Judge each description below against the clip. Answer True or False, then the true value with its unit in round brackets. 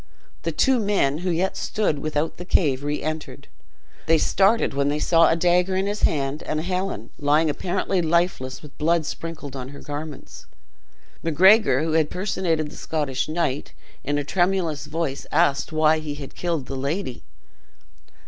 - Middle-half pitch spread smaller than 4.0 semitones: True (3.5 semitones)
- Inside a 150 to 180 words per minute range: True (165 wpm)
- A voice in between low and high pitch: True (155 Hz)